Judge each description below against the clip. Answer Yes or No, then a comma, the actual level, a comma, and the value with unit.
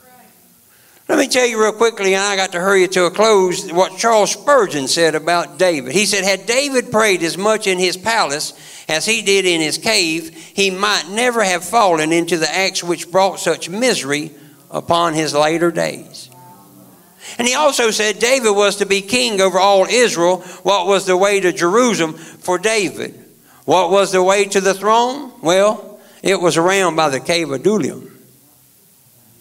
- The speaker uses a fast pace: No, average, 180 wpm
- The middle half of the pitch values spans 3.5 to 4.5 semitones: Yes, average, 3.9 semitones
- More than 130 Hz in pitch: Yes, high, 190 Hz